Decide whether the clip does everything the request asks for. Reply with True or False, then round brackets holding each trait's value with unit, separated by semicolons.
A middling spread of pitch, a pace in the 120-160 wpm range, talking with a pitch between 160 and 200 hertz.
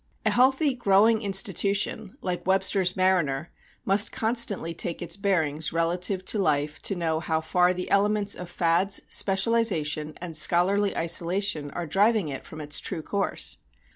True (3.5 semitones; 145 wpm; 185 Hz)